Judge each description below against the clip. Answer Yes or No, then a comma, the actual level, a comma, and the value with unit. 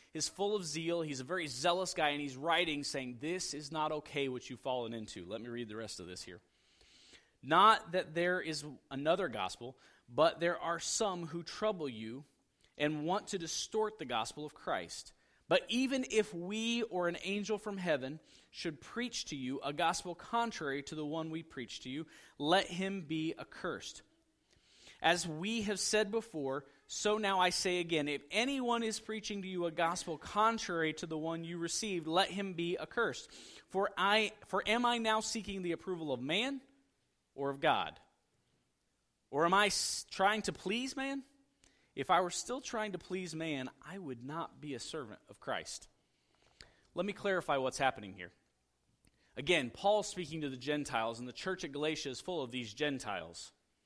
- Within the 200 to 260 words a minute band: No, average, 185 wpm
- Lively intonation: Yes, wide, 5.7 semitones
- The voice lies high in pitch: No, medium, 170 Hz